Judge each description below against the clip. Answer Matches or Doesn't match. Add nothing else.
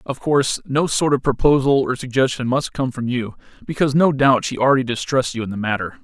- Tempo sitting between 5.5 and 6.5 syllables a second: Matches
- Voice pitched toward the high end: Doesn't match